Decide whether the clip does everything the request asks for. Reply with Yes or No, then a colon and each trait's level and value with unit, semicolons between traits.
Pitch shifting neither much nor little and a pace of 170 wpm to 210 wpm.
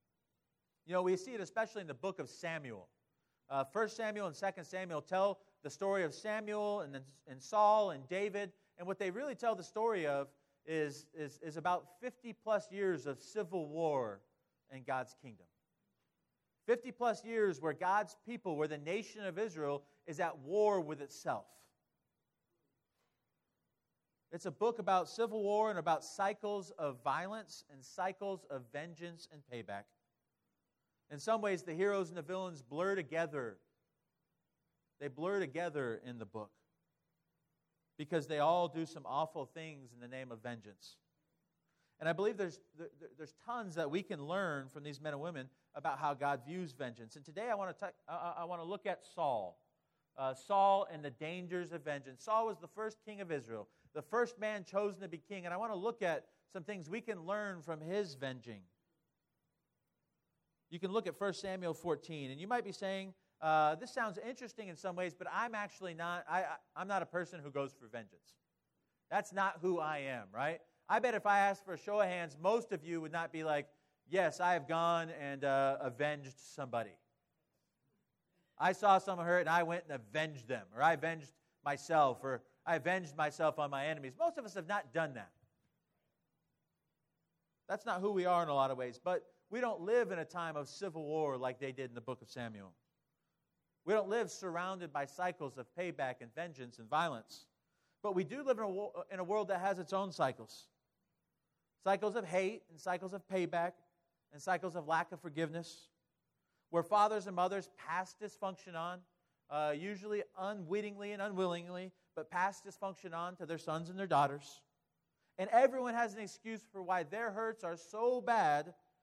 Yes: average, 4.7 semitones; average, 185 wpm